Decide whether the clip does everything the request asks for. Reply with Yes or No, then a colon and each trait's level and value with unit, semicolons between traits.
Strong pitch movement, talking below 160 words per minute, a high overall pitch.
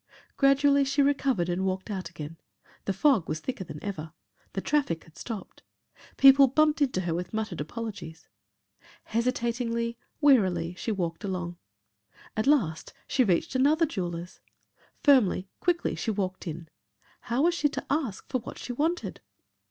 Yes: wide, 7.5 semitones; average, 150 wpm; high, 220 Hz